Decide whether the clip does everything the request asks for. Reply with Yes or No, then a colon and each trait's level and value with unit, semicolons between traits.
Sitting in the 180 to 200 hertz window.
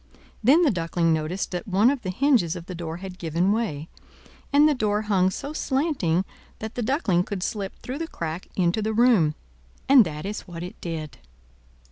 Yes: high, 190 Hz